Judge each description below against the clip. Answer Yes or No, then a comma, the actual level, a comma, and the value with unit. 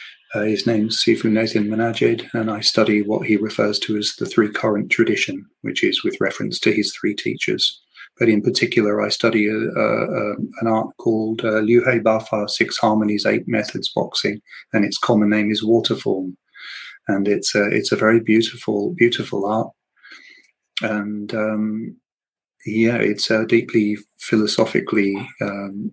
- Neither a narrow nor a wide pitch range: No, narrow, 1.3 semitones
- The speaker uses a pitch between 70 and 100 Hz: No, low, 110 Hz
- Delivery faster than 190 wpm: No, average, 155 wpm